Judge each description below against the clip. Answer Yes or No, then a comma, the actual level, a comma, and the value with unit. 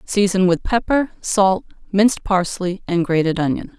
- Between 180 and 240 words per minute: No, average, 145 wpm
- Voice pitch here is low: No, high, 190 Hz